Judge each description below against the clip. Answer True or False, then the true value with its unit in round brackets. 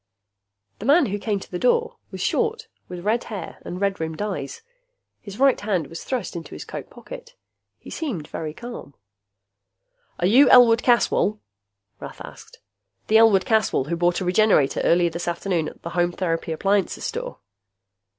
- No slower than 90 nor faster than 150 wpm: False (170 wpm)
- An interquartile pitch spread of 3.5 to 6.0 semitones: True (5.4 semitones)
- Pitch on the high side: True (195 Hz)